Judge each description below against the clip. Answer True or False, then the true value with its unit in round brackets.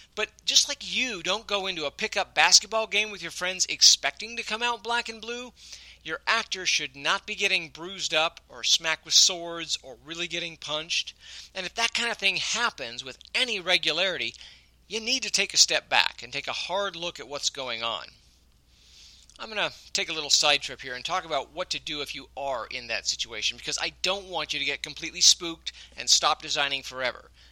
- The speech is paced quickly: True (210 wpm)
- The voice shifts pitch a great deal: True (5.8 semitones)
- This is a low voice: False (170 Hz)